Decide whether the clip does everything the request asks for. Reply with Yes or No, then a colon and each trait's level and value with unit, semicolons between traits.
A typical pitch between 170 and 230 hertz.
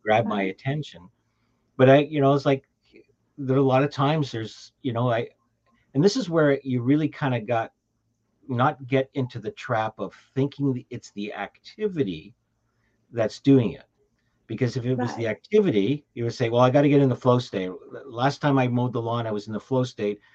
No: low, 125 Hz